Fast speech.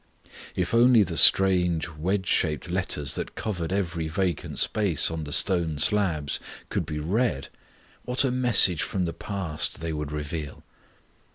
No: average, 150 wpm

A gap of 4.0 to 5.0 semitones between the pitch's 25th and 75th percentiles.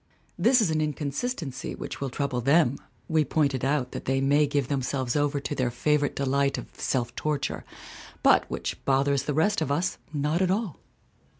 No: narrow, 2.4 semitones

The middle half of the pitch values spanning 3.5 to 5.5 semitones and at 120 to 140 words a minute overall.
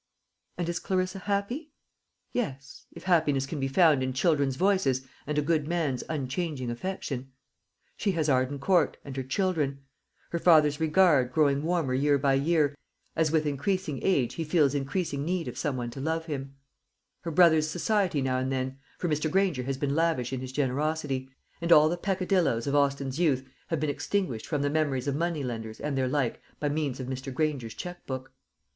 No: average, 4.0 semitones; average, 185 wpm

